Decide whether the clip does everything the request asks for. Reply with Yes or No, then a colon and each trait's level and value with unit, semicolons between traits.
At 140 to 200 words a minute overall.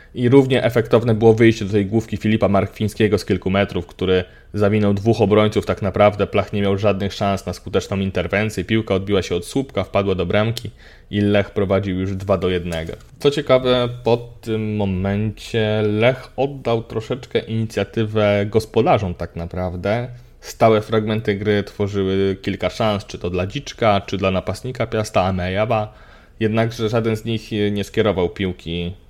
Yes: average, 155 wpm